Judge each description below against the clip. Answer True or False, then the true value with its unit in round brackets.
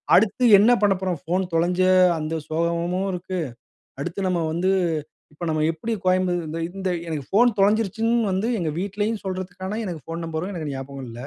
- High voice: False (180 Hz)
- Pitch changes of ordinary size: True (3.1 semitones)